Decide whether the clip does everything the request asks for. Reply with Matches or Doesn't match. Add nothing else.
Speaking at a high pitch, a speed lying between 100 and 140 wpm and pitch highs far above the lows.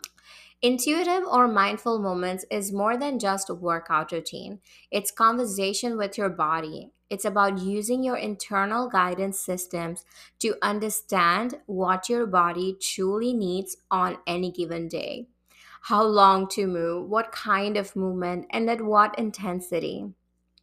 Doesn't match